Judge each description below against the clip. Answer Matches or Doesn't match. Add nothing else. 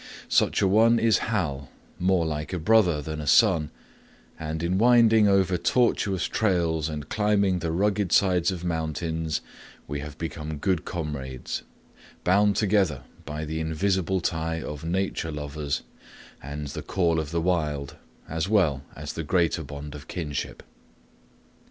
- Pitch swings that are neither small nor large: Matches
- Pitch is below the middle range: Matches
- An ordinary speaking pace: Matches